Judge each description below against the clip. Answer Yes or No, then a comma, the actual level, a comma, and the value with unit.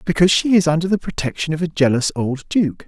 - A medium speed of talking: No, fast, 230 wpm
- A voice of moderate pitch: Yes, medium, 160 Hz